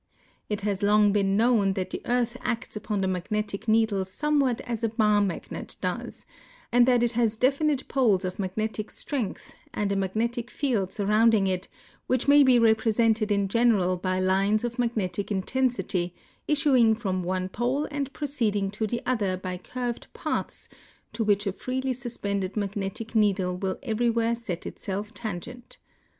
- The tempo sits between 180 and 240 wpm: No, average, 160 wpm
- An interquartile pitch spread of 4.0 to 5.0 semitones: No, average, 3.6 semitones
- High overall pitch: Yes, high, 215 Hz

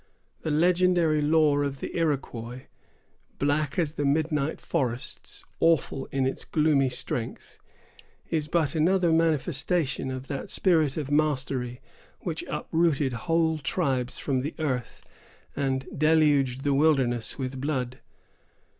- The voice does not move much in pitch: No, average, 3.3 semitones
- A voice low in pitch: No, medium, 145 Hz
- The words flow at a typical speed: No, slow, 120 wpm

